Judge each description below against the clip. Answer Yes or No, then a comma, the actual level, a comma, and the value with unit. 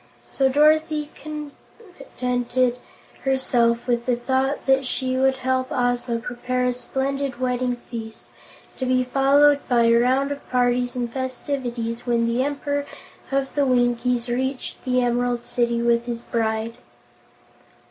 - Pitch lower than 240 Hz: No, very high, 250 Hz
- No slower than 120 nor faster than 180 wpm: Yes, slow, 135 wpm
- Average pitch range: No, narrow, 1.9 semitones